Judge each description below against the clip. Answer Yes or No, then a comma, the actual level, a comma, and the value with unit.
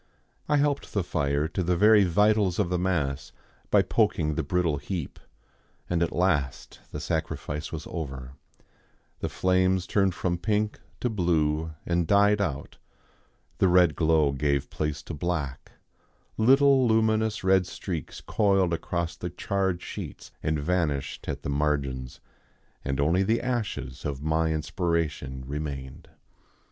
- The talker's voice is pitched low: Yes, very low, 85 Hz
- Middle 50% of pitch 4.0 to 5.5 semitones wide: Yes, average, 4.6 semitones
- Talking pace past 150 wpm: No, average, 140 wpm